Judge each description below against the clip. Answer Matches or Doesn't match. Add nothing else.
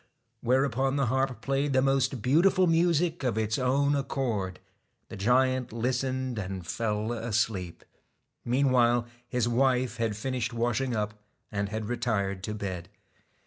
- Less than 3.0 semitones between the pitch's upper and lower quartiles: Doesn't match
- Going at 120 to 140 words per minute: Matches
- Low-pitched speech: Matches